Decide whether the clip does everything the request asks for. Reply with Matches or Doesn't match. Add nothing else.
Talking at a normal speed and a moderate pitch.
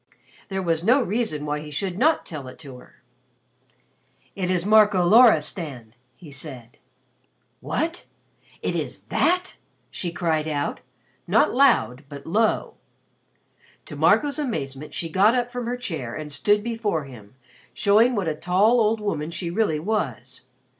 Matches